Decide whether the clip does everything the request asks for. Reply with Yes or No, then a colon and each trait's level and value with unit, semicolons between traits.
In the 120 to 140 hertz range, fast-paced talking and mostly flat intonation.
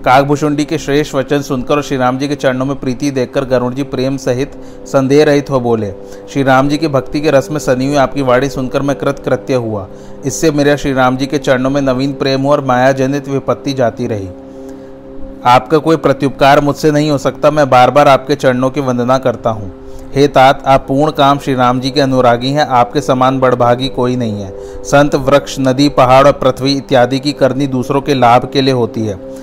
Yes: low, 135 Hz; fast, 210 wpm; narrow, 1.9 semitones